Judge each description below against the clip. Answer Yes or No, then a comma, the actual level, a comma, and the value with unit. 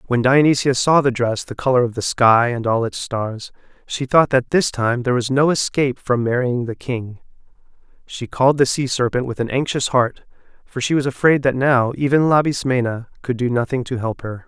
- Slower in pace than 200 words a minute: No, fast, 205 wpm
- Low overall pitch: Yes, low, 125 Hz